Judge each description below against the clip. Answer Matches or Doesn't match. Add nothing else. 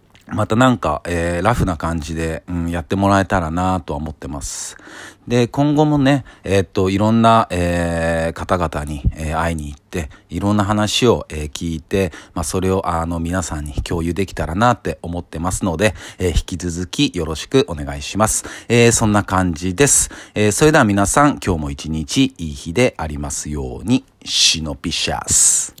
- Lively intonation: Doesn't match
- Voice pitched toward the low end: Matches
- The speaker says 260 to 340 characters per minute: Doesn't match